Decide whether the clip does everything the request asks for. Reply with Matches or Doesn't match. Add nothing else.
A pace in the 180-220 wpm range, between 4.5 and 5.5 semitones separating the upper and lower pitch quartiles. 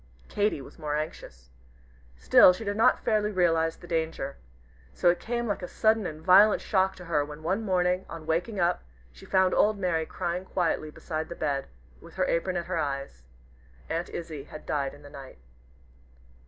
Doesn't match